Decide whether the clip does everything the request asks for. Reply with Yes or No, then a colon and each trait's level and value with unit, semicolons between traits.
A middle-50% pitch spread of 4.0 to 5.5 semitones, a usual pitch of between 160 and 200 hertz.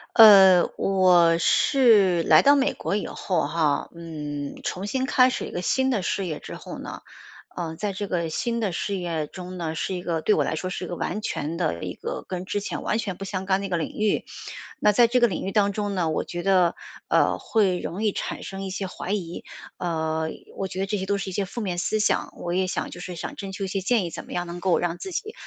No: average, 3.0 semitones; medium, 185 Hz